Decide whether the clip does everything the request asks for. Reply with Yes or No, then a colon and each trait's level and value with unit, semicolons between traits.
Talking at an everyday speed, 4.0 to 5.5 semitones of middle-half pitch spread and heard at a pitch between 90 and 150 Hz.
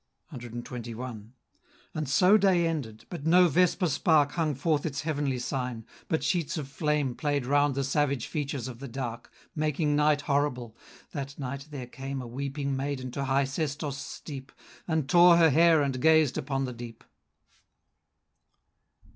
No: average, 155 wpm; average, 3.0 semitones; medium, 140 Hz